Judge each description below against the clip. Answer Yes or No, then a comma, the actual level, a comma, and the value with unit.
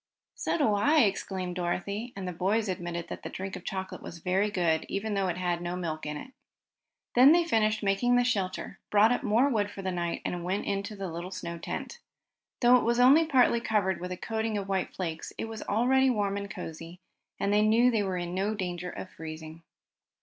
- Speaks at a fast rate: Yes, fast, 220 wpm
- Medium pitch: No, high, 195 Hz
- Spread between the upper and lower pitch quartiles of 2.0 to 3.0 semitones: No, average, 3.8 semitones